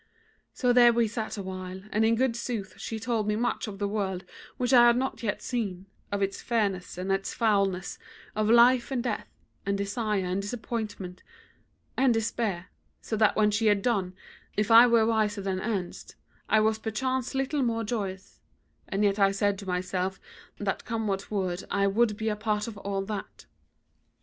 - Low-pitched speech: No, high, 210 Hz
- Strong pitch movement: No, average, 2.9 semitones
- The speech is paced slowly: No, average, 185 wpm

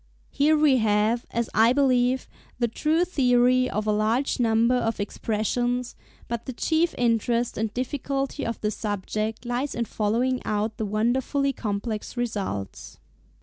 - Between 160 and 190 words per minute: No, average, 145 wpm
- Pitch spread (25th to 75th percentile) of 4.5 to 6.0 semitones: No, average, 2.9 semitones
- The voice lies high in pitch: Yes, high, 235 Hz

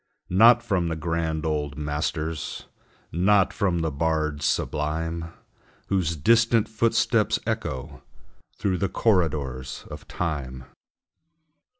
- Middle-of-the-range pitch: No, very low, 80 Hz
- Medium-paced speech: No, slow, 100 wpm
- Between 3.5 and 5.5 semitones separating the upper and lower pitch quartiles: Yes, average, 4.1 semitones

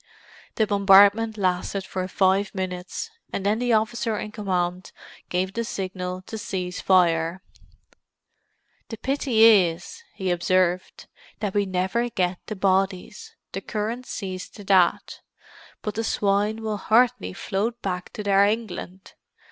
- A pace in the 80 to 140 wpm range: Yes, slow, 135 wpm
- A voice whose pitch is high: Yes, high, 195 Hz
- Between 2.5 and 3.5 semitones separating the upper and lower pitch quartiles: Yes, average, 2.9 semitones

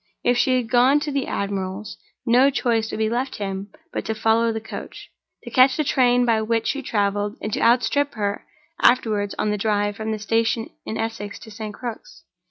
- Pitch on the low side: No, high, 225 Hz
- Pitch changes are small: No, average, 3.0 semitones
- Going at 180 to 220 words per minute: Yes, average, 200 wpm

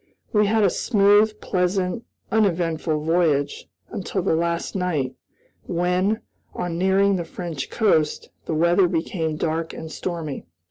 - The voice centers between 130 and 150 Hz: No, medium, 175 Hz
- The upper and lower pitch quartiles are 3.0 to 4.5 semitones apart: Yes, average, 3.3 semitones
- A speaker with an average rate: No, slow, 130 wpm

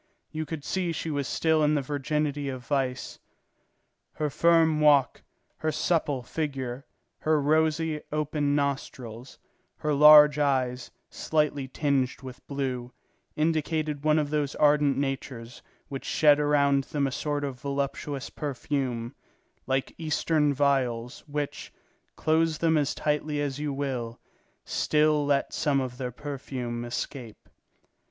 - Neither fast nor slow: No, slow, 130 wpm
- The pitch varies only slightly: Yes, narrow, 2.3 semitones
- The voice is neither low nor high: Yes, medium, 145 Hz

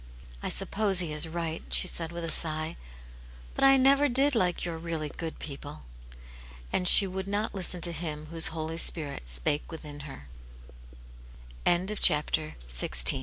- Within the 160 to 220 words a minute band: No, slow, 135 wpm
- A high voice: No, medium, 170 Hz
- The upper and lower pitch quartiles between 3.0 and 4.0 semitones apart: Yes, average, 3.5 semitones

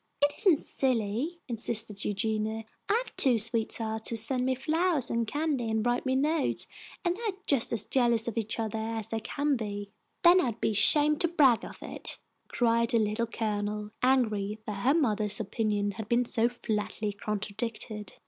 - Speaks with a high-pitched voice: Yes, high, 230 Hz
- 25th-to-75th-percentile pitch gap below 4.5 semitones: Yes, average, 3.7 semitones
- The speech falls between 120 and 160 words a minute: No, average, 175 wpm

